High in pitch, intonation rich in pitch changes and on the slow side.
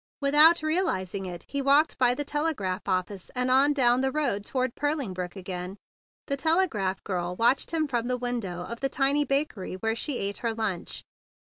No: high, 245 Hz; wide, 6.8 semitones; average, 185 wpm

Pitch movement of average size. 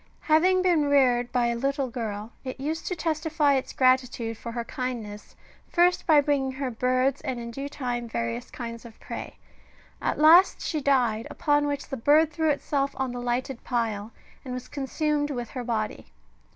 Yes: average, 3.5 semitones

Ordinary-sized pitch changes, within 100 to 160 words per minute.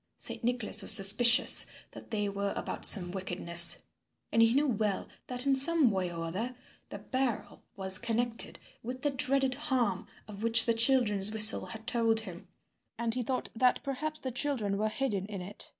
No: average, 4.1 semitones; average, 180 wpm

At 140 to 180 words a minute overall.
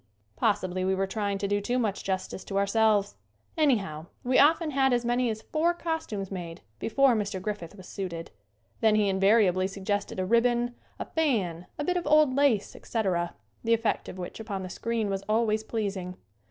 No: average, 190 wpm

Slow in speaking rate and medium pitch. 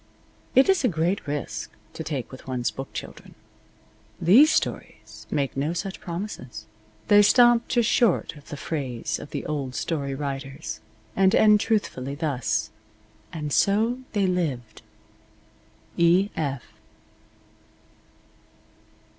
Yes: slow, 120 wpm; medium, 160 Hz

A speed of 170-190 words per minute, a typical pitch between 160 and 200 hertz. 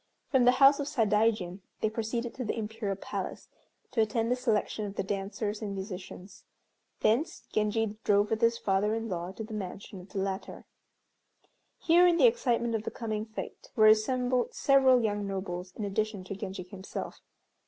No: average, 175 wpm; high, 215 Hz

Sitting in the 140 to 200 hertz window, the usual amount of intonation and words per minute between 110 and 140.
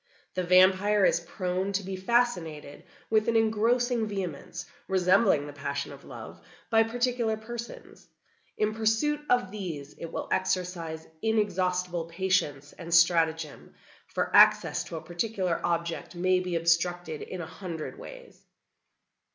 Yes: medium, 185 Hz; average, 4.5 semitones; slow, 135 wpm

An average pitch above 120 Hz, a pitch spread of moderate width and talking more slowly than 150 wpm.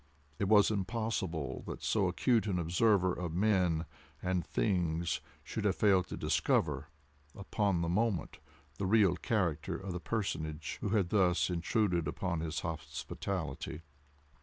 No: very low, 90 Hz; average, 3.5 semitones; slow, 135 wpm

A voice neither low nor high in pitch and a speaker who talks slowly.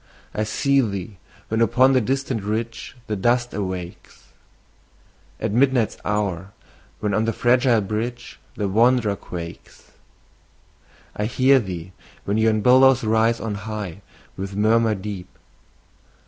No: low, 110 Hz; slow, 125 wpm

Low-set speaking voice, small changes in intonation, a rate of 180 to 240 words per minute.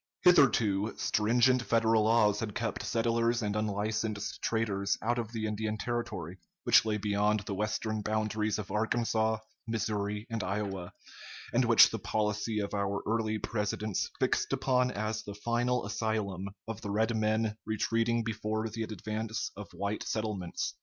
No: low, 110 Hz; narrow, 1.5 semitones; average, 145 wpm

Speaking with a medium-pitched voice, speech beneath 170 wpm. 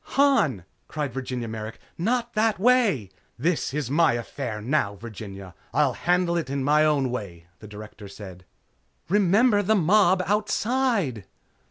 Yes: medium, 150 Hz; average, 140 wpm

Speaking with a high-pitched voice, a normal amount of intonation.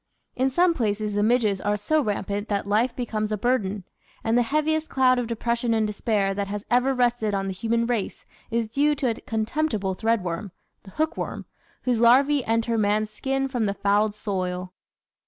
Yes: high, 225 Hz; average, 3.4 semitones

